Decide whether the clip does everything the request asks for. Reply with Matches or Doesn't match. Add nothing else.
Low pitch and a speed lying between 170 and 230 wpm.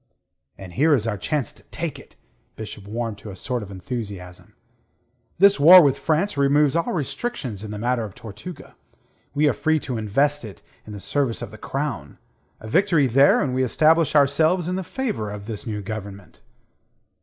Matches